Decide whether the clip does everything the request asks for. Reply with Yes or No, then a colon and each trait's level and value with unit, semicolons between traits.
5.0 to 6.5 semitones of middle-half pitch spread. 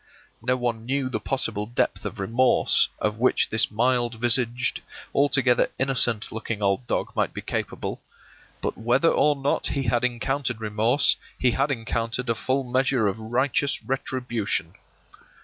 No: average, 2.8 semitones